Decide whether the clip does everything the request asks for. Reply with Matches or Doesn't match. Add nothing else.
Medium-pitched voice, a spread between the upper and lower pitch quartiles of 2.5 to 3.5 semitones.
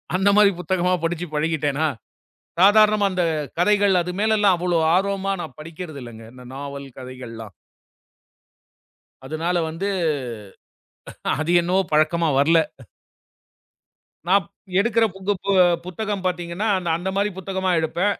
Doesn't match